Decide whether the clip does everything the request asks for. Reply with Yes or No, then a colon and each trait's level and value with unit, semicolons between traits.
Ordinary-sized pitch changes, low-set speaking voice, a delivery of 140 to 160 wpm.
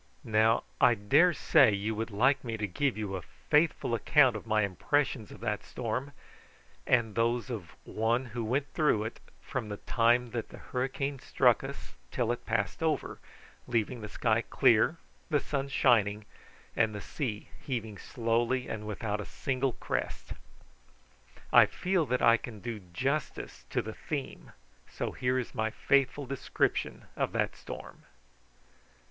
Yes: average, 3.4 semitones; low, 120 Hz; average, 155 wpm